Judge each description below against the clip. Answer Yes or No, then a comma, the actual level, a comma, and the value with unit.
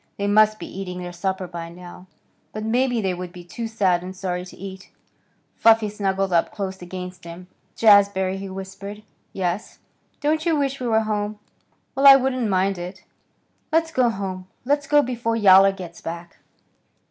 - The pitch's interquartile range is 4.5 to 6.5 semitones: No, average, 3.7 semitones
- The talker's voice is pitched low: No, high, 195 Hz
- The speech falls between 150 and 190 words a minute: Yes, average, 170 wpm